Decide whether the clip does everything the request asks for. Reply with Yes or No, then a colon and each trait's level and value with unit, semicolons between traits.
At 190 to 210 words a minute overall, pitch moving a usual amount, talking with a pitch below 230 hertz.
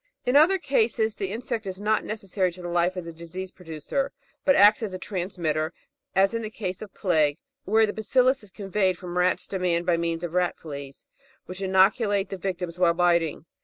Yes: average, 200 wpm; average, 3.5 semitones; medium, 185 Hz